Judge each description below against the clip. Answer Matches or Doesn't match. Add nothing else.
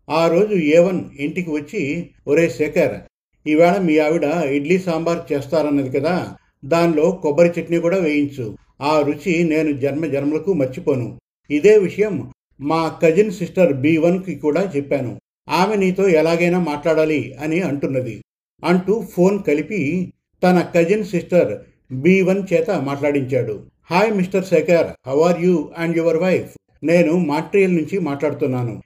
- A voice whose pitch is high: Doesn't match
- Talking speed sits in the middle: Doesn't match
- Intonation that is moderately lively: Matches